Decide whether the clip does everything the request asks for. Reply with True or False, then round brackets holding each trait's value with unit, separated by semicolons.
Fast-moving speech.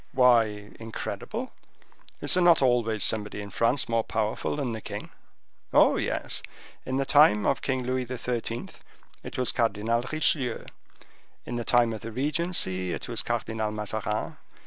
False (150 wpm)